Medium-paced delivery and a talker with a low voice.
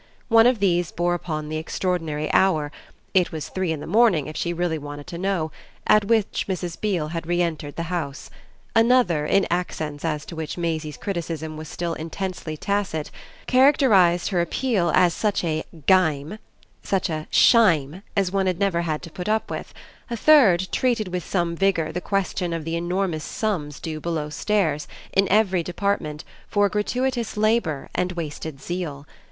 No: average, 170 wpm; medium, 175 Hz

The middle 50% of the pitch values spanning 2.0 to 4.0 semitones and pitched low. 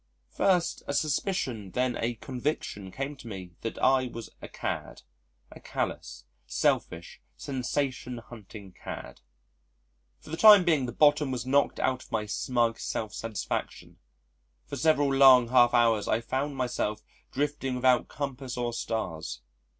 Yes: average, 3.5 semitones; low, 125 Hz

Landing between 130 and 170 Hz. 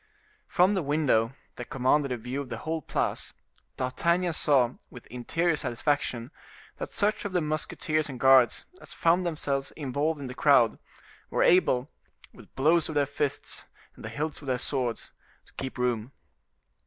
Yes: medium, 140 Hz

